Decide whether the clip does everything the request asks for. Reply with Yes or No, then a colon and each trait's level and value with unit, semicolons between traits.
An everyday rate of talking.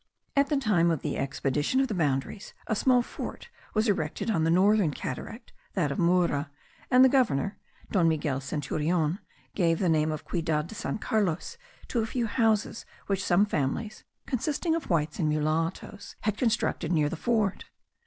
Yes: average, 175 wpm